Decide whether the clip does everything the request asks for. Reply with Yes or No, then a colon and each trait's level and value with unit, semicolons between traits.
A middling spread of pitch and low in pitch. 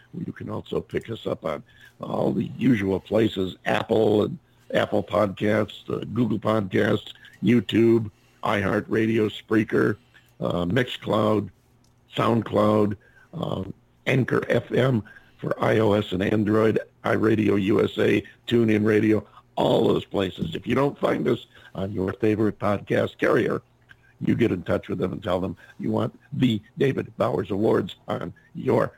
No: narrow, 1.5 semitones; low, 105 Hz